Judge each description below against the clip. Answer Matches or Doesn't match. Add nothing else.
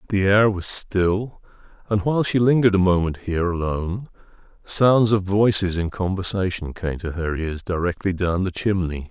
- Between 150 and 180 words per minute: Matches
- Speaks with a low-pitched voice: Matches